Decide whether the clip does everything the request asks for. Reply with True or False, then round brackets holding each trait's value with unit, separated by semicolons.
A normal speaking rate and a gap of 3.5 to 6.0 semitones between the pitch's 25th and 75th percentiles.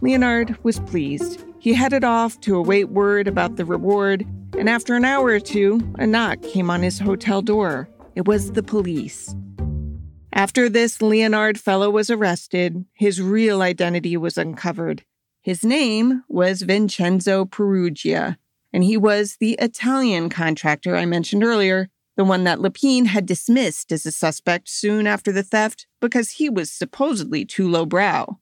True (155 wpm; 4.4 semitones)